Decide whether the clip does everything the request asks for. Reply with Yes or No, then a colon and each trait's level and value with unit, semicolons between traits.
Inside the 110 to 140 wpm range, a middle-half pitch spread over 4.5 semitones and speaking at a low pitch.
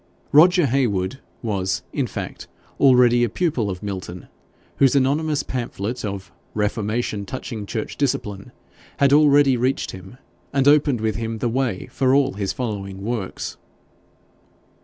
Yes: slow, 135 wpm; average, 5.1 semitones; low, 120 Hz